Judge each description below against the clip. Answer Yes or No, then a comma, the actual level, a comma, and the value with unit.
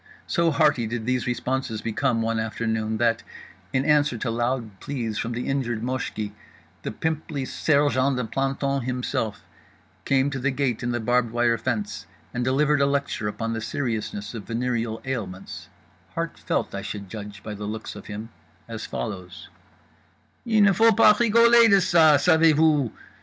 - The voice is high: No, low, 125 Hz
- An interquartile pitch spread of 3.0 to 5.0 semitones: Yes, average, 4.2 semitones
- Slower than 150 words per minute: No, average, 165 wpm